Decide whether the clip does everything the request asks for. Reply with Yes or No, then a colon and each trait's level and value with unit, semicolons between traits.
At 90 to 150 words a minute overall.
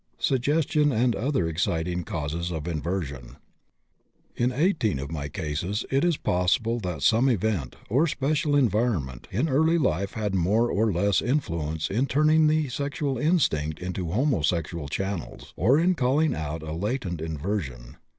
Yes: average, 145 wpm